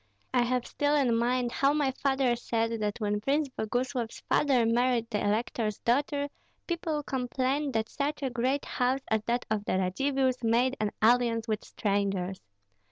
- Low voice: No, high, 245 Hz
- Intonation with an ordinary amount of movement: Yes, average, 3.2 semitones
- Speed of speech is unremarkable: Yes, average, 165 wpm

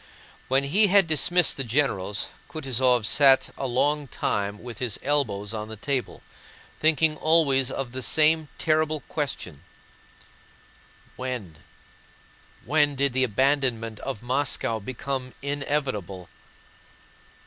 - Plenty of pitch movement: No, average, 4.4 semitones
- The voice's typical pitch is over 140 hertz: No, low, 135 Hz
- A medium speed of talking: No, slow, 115 wpm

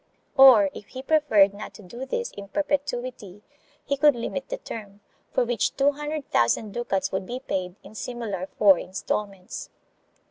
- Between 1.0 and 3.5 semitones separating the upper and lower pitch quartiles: No, wide, 5.5 semitones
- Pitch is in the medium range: No, high, 230 Hz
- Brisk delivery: No, average, 165 wpm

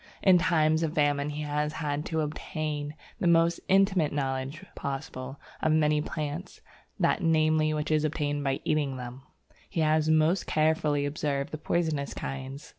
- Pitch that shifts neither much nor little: No, narrow, 1.6 semitones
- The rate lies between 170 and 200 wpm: No, average, 160 wpm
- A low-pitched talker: No, medium, 150 Hz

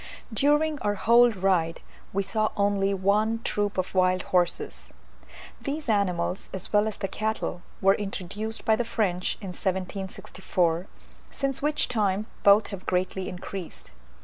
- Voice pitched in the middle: No, high, 200 Hz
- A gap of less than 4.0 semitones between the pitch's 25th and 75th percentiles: Yes, average, 2.8 semitones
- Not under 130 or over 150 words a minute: Yes, average, 140 wpm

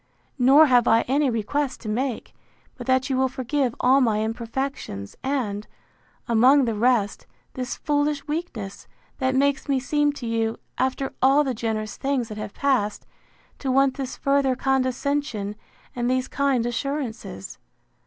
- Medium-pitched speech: No, very high, 260 Hz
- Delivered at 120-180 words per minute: Yes, average, 150 wpm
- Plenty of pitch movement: No, average, 3.4 semitones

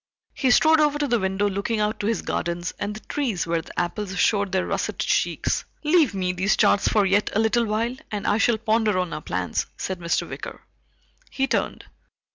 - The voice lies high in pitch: Yes, high, 210 Hz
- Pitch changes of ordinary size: Yes, average, 3.5 semitones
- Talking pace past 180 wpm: Yes, fast, 205 wpm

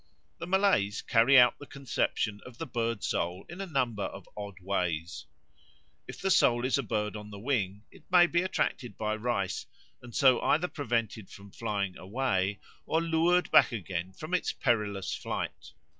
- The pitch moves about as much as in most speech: No, wide, 6.1 semitones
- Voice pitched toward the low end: Yes, low, 115 Hz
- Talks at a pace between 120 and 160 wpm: No, average, 175 wpm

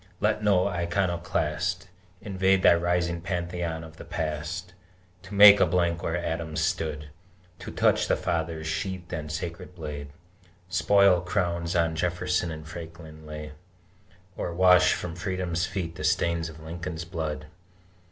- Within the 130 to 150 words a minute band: Yes, average, 140 wpm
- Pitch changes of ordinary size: No, narrow, 2.1 semitones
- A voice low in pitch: Yes, very low, 85 Hz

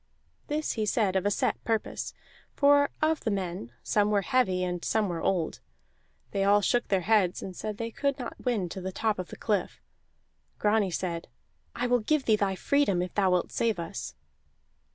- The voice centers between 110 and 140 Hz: No, high, 205 Hz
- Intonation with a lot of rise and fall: No, average, 4.0 semitones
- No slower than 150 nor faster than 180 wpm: No, average, 195 wpm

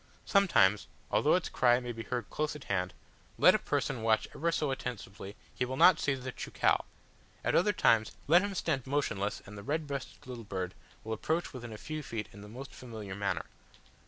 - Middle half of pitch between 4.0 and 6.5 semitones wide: Yes, wide, 5.6 semitones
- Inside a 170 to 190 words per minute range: No, average, 200 wpm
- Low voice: Yes, low, 125 Hz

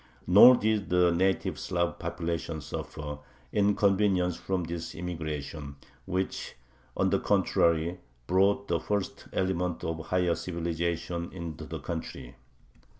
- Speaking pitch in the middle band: No, very low, 85 Hz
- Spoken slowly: Yes, slow, 120 wpm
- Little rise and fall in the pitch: Yes, narrow, 2.3 semitones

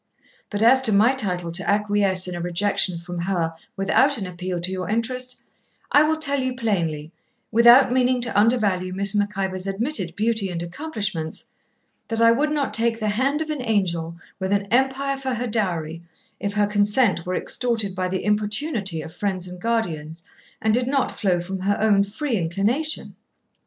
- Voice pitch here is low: No, high, 205 Hz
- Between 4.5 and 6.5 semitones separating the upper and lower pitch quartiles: Yes, average, 4.8 semitones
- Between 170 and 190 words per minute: Yes, average, 180 wpm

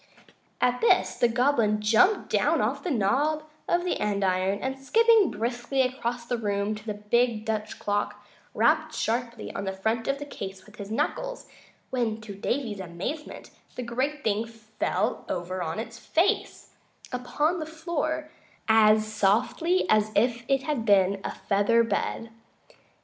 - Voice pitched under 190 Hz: No, high, 230 Hz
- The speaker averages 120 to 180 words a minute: Yes, average, 155 wpm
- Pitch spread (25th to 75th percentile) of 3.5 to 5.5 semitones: Yes, average, 4.7 semitones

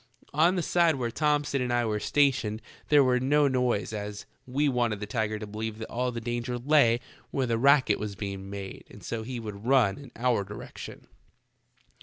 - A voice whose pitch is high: No, low, 120 Hz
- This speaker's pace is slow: No, average, 195 wpm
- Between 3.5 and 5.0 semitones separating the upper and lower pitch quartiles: Yes, average, 4.2 semitones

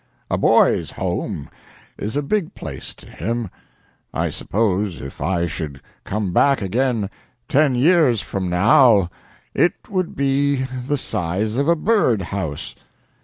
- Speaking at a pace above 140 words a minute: No, slow, 135 wpm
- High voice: No, low, 115 Hz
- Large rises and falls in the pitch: Yes, wide, 6.7 semitones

